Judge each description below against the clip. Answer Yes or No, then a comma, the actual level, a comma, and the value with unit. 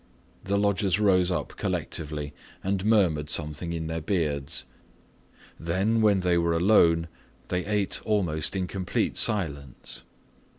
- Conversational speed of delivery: No, slow, 125 wpm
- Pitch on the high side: No, very low, 90 Hz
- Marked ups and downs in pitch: No, average, 3.7 semitones